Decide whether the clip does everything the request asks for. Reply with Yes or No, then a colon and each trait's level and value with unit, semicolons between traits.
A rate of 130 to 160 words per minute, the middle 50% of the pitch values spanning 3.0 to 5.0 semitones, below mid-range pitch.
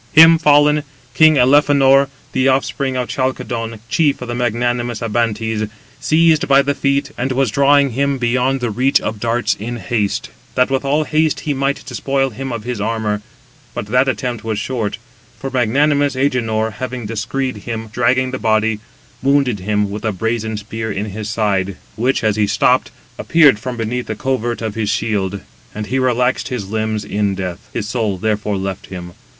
No: average, 175 wpm; average, 3.8 semitones; low, 120 Hz